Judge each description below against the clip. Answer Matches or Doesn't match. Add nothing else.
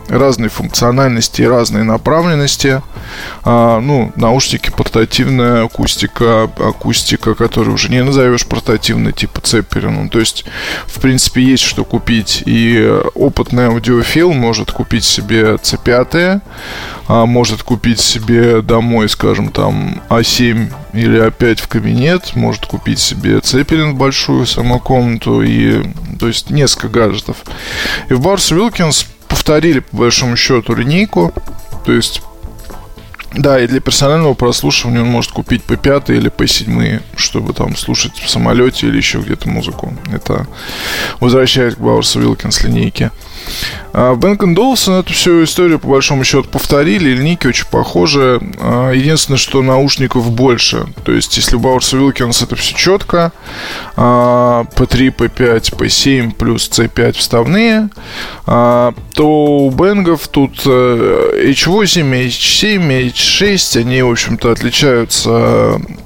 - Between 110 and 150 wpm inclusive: Matches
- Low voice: Matches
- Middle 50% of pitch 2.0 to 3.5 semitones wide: Matches